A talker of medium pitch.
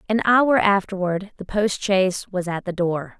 No: high, 195 Hz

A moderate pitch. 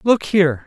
Yes: medium, 180 Hz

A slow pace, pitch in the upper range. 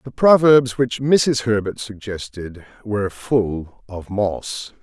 No: slow, 125 wpm; low, 110 Hz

